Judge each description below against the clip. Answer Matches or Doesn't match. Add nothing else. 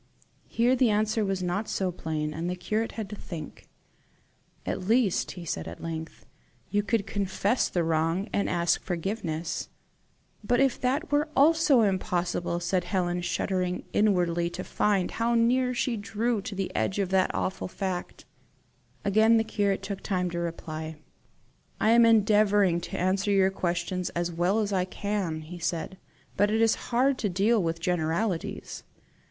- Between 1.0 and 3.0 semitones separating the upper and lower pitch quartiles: Doesn't match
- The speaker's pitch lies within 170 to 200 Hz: Matches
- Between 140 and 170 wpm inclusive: Matches